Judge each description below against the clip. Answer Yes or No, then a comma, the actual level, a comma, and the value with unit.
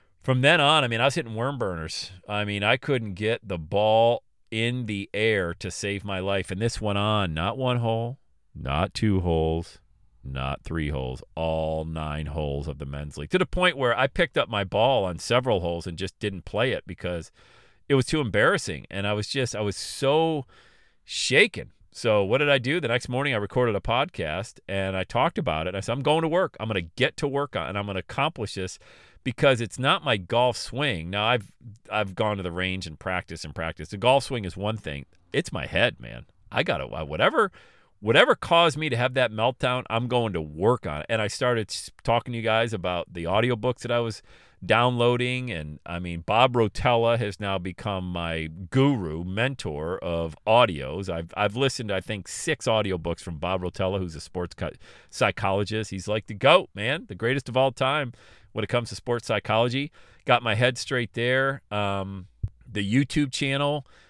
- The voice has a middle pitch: No, low, 105 Hz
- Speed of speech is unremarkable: No, fast, 210 wpm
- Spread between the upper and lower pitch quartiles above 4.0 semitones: Yes, wide, 5.4 semitones